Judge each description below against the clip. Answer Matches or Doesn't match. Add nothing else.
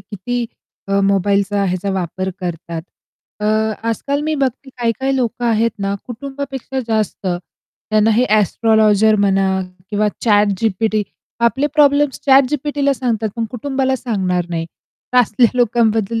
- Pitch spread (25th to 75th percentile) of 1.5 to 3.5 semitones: Doesn't match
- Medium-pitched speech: Doesn't match